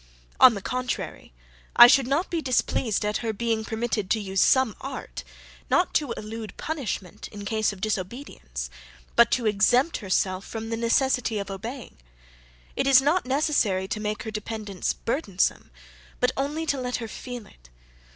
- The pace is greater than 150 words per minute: Yes, average, 160 wpm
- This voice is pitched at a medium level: No, high, 225 Hz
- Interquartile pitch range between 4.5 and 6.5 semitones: No, average, 4.1 semitones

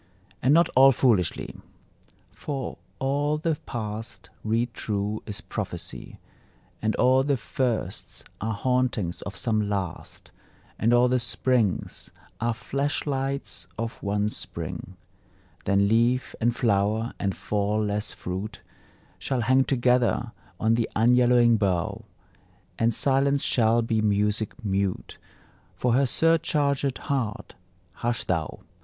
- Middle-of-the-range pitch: No, low, 115 Hz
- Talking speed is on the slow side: Yes, slow, 120 wpm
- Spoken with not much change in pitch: No, average, 3.7 semitones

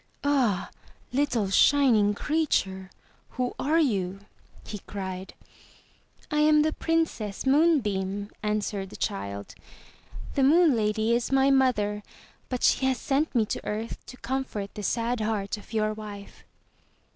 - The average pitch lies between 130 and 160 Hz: No, high, 225 Hz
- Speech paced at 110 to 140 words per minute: Yes, slow, 135 wpm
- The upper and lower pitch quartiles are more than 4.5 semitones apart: Yes, average, 5.1 semitones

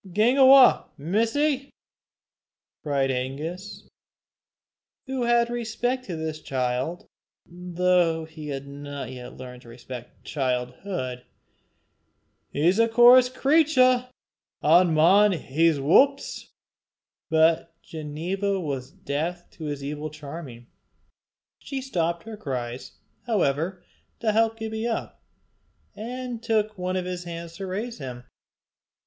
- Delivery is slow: Yes, slow, 115 wpm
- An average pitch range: No, wide, 7.8 semitones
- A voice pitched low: No, medium, 175 Hz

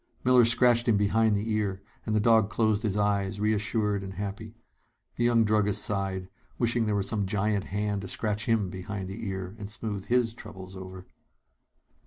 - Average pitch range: No, narrow, 2.2 semitones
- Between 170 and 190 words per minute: Yes, average, 180 wpm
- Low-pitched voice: Yes, low, 105 Hz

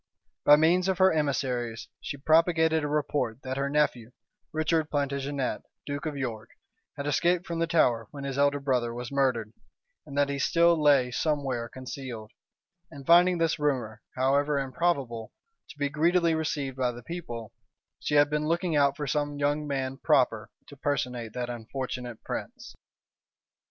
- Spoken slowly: No, average, 160 wpm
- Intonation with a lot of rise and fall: No, average, 3.4 semitones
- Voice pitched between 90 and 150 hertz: Yes, medium, 140 Hz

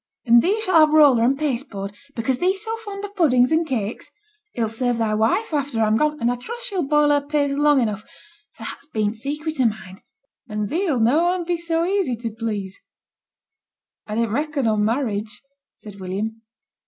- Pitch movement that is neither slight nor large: No, wide, 6.1 semitones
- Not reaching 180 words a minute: No, average, 200 wpm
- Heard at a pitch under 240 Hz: No, very high, 260 Hz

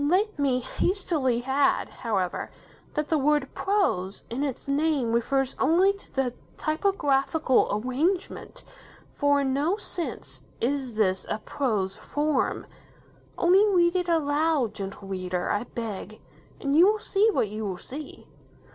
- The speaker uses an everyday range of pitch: No, wide, 6.1 semitones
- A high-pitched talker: Yes, very high, 280 Hz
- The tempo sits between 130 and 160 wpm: Yes, average, 140 wpm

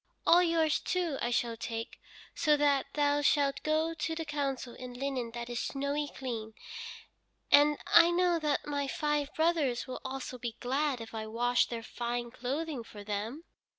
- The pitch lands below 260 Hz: No, very high, 275 Hz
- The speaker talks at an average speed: Yes, average, 170 wpm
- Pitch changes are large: No, average, 3.9 semitones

